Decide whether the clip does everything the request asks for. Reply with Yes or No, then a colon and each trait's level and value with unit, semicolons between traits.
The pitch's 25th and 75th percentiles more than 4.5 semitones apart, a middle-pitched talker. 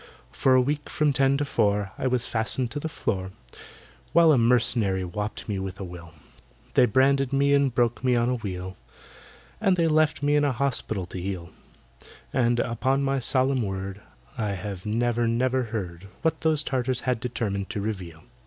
No: wide, 5.5 semitones; low, 120 Hz